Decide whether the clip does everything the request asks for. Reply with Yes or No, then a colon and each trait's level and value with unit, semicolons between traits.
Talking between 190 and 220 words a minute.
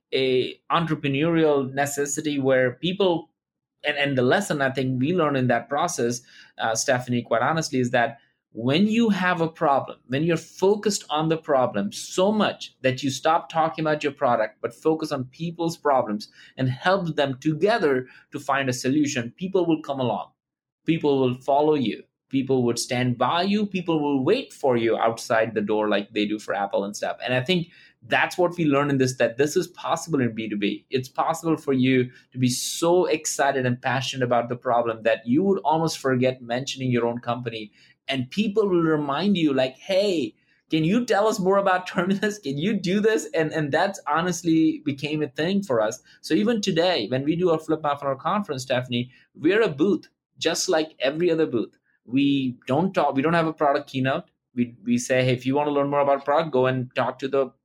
Yes: average, 200 wpm